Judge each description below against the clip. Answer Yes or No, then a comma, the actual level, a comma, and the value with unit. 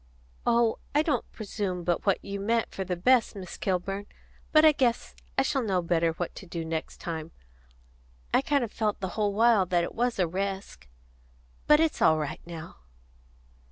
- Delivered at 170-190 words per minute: Yes, average, 180 wpm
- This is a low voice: No, high, 195 Hz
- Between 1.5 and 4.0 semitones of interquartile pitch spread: No, average, 5.2 semitones